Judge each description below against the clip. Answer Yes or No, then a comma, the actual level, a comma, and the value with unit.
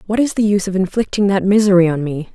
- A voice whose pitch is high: Yes, high, 195 Hz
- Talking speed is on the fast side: Yes, fast, 255 wpm